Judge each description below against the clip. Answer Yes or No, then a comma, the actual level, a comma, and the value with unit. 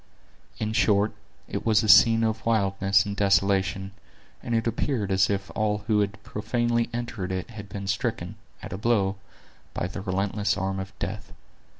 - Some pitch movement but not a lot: No, narrow, 2.3 semitones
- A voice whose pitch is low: Yes, low, 100 Hz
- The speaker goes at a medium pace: Yes, average, 170 wpm